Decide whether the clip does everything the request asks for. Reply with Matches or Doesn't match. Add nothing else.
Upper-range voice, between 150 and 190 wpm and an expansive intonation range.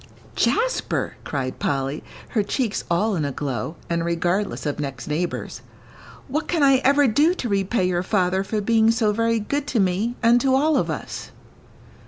Matches